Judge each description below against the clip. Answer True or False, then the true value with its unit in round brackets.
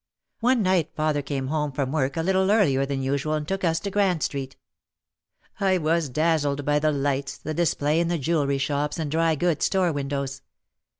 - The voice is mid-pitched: True (155 Hz)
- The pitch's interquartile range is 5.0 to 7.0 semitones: False (3.4 semitones)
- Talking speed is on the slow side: False (190 wpm)